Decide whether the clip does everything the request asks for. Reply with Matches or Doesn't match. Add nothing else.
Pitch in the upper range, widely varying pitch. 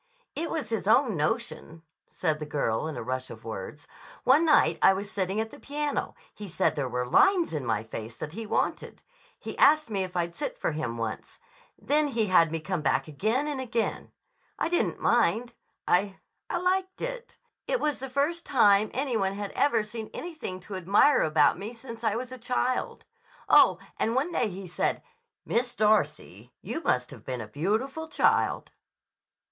Matches